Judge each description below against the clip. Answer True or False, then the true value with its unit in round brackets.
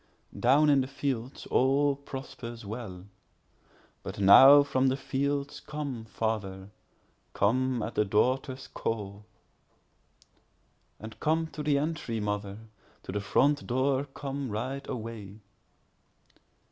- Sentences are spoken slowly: True (100 wpm)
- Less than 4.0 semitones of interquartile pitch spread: False (4.7 semitones)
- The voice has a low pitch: True (130 Hz)